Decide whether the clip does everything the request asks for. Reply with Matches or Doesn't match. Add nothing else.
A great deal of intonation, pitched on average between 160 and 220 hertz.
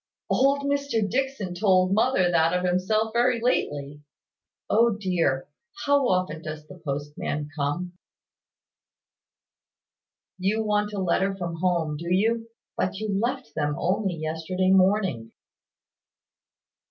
Doesn't match